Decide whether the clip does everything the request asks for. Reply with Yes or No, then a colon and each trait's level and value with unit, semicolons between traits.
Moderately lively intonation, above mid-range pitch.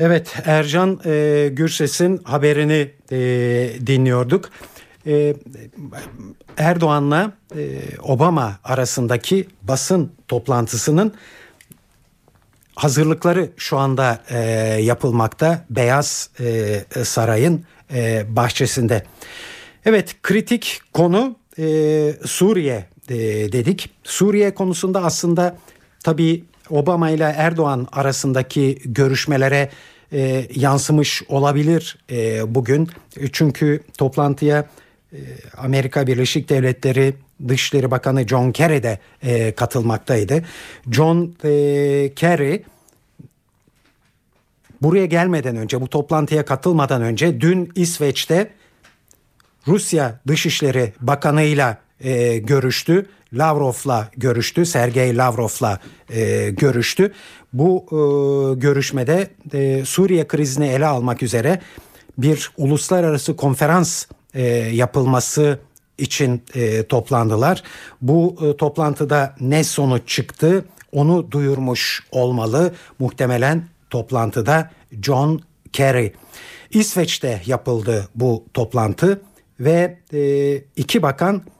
No: average, 4.3 semitones; medium, 140 Hz